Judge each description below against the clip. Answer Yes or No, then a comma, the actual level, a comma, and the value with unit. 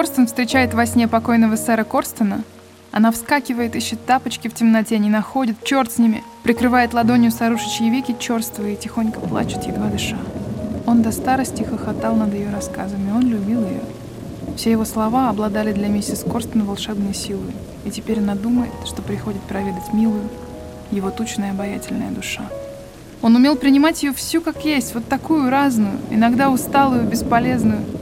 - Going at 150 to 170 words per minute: Yes, fast, 155 wpm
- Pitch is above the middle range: Yes, high, 230 Hz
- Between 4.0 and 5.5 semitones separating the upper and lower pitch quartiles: No, average, 2.7 semitones